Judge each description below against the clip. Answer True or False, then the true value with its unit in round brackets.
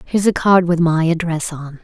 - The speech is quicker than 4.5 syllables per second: True (5.2 syllables/s)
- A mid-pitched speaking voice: True (170 Hz)